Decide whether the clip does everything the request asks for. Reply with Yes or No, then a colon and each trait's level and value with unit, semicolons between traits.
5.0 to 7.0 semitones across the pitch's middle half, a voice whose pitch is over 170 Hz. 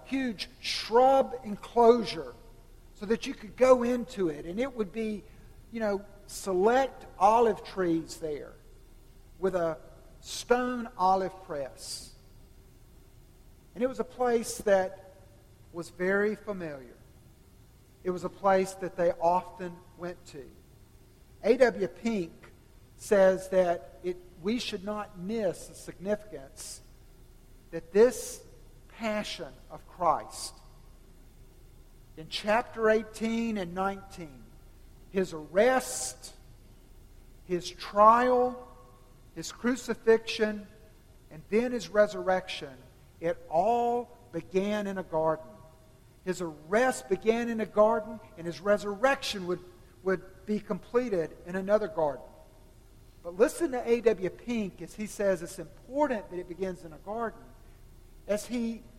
Yes: wide, 5.4 semitones; high, 190 Hz